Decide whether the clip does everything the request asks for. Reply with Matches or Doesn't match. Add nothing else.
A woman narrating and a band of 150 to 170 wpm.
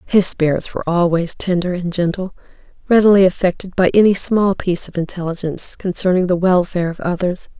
Matches